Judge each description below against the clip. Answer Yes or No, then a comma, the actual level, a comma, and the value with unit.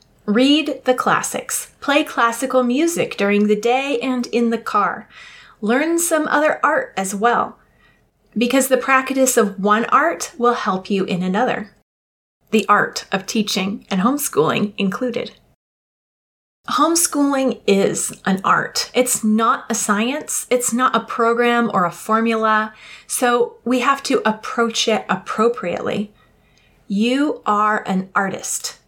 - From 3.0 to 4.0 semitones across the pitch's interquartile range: Yes, average, 3.4 semitones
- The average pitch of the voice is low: No, high, 235 Hz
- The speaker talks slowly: Yes, slow, 130 wpm